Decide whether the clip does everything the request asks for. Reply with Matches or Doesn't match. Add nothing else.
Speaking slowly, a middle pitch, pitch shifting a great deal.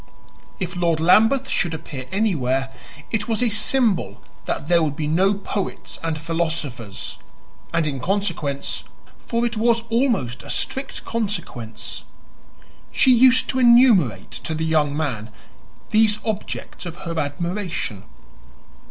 Matches